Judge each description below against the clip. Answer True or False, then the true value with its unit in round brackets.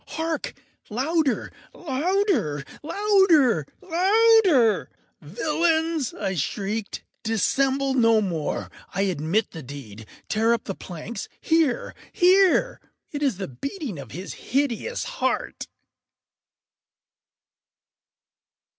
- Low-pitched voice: False (255 Hz)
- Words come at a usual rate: False (85 wpm)